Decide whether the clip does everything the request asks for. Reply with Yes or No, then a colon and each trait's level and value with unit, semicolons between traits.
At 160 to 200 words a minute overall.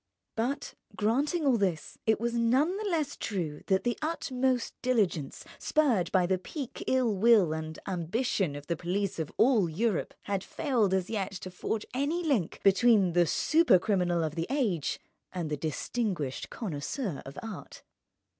No: average, 150 wpm